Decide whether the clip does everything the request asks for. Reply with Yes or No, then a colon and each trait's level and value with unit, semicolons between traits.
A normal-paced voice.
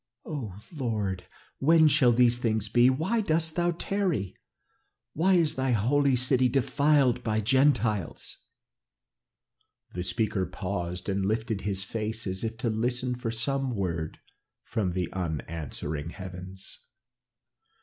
No: slow, 130 wpm